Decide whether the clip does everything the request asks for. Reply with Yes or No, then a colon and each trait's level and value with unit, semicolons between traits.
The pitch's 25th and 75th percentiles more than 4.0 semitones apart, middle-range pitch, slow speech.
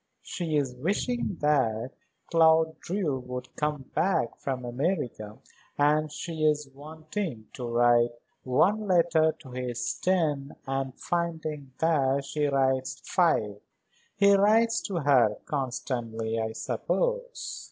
Yes: average, 4.9 semitones; medium, 145 Hz; slow, 120 wpm